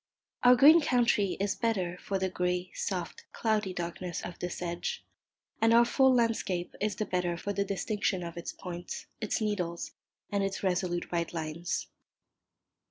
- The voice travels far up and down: No, average, 3.5 semitones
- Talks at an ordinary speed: Yes, average, 165 wpm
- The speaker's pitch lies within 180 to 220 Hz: Yes, high, 190 Hz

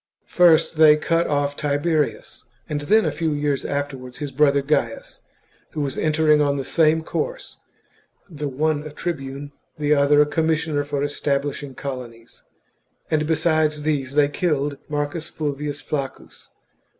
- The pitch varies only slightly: Yes, narrow, 1.7 semitones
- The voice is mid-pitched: Yes, medium, 145 Hz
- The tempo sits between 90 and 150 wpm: Yes, average, 145 wpm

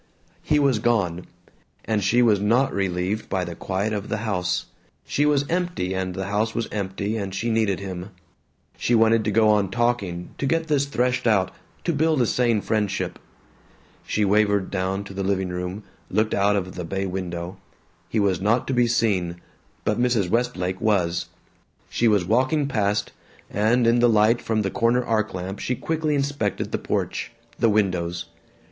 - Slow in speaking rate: No, average, 180 wpm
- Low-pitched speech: Yes, low, 105 Hz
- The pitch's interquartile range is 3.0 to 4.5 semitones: Yes, average, 3.9 semitones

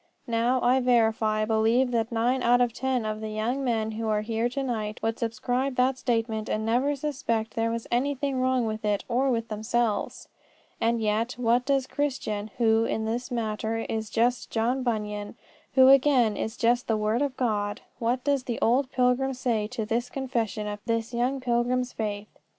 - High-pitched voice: Yes, high, 235 Hz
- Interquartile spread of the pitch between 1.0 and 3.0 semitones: Yes, narrow, 2.4 semitones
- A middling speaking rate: Yes, average, 185 wpm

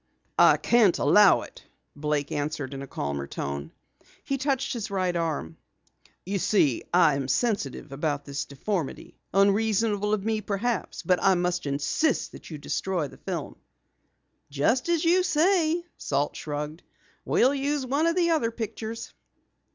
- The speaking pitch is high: Yes, high, 195 Hz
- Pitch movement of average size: No, wide, 8.8 semitones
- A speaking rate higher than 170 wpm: No, average, 150 wpm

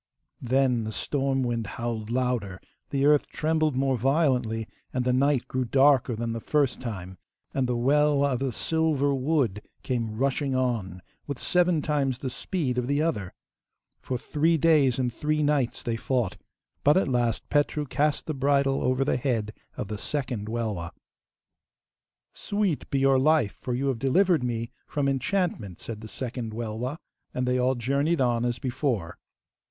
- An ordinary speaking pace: Yes, average, 165 wpm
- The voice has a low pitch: Yes, low, 130 Hz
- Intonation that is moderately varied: Yes, average, 3.5 semitones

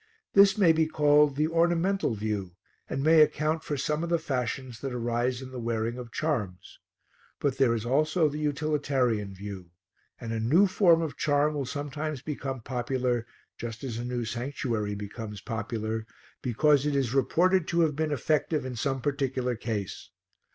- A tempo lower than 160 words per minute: No, average, 170 wpm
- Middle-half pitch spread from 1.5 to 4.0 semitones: No, average, 4.7 semitones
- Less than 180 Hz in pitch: Yes, low, 135 Hz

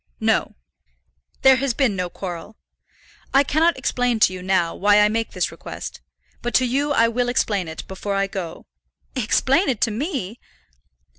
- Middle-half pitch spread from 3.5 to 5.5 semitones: Yes, average, 5.2 semitones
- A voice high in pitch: Yes, high, 225 Hz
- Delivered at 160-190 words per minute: Yes, average, 165 wpm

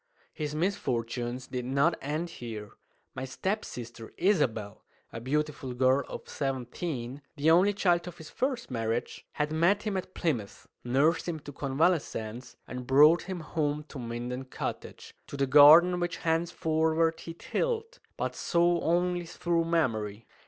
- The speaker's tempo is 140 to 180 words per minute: Yes, average, 145 wpm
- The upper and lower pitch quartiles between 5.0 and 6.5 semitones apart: Yes, wide, 5.4 semitones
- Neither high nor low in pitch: Yes, medium, 150 Hz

